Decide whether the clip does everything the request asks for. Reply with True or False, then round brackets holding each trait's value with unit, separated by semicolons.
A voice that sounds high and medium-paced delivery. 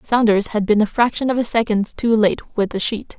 False (220 Hz; 245 wpm)